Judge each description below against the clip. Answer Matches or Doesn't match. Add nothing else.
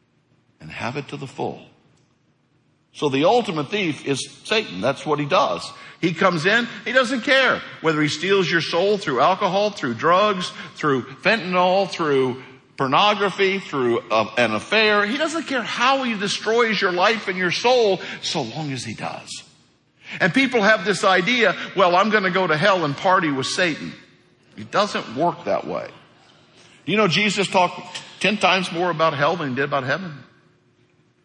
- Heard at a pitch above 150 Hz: Matches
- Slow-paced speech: Doesn't match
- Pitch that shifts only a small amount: Doesn't match